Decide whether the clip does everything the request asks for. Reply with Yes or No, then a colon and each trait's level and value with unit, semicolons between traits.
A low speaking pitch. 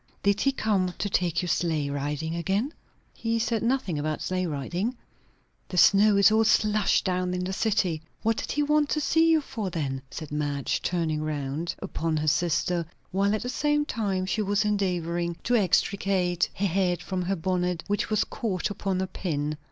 No: medium, 185 Hz